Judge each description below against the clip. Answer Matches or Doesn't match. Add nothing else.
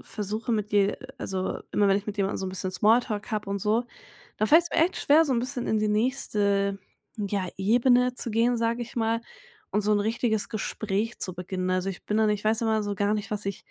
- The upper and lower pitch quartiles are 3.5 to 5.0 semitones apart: Doesn't match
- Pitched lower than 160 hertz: Doesn't match